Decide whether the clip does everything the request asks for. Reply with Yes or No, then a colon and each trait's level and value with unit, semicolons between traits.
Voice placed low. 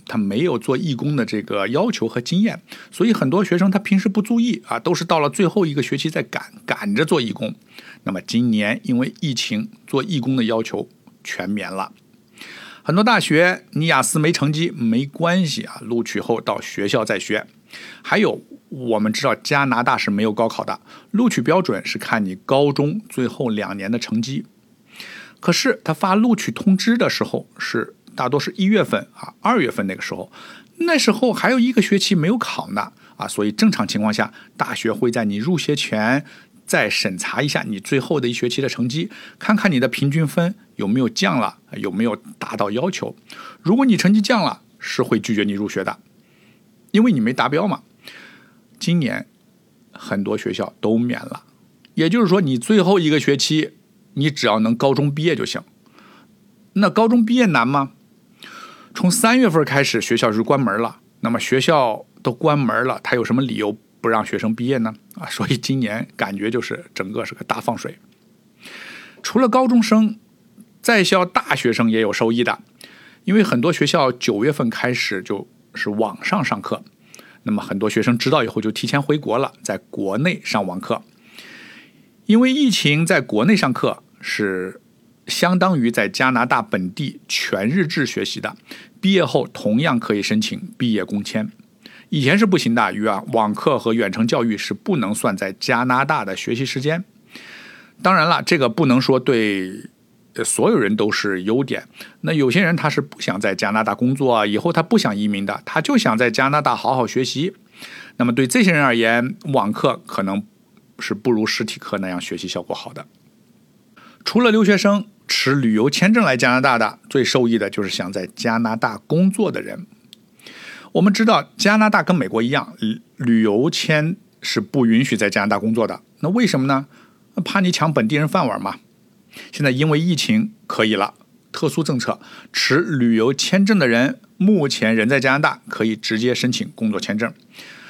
No: medium, 155 Hz